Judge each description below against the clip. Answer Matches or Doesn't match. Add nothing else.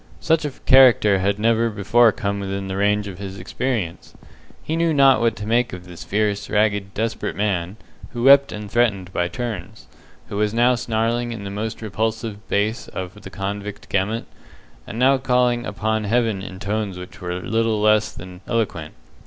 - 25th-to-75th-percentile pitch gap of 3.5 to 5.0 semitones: Doesn't match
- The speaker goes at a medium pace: Matches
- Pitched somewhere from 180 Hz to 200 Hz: Doesn't match